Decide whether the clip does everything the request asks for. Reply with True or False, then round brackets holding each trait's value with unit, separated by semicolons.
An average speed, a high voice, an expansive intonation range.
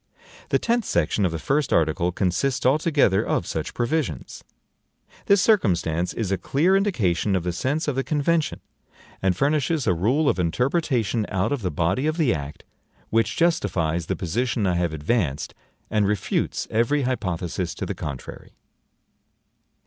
False (155 wpm; 110 Hz; 8.7 semitones)